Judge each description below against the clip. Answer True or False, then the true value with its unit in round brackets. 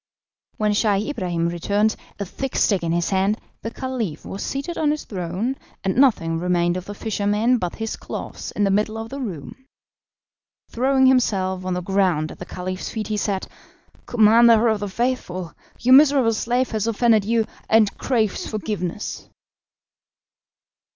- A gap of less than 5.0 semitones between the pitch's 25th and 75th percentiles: True (4.1 semitones)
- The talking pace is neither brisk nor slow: True (160 wpm)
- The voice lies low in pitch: False (210 Hz)